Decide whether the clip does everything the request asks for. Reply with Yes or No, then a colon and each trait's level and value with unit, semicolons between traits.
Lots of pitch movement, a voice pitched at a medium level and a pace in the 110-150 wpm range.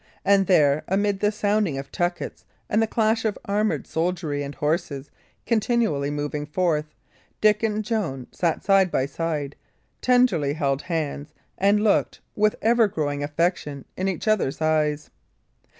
Yes: wide, 6.1 semitones; medium, 175 Hz; average, 145 wpm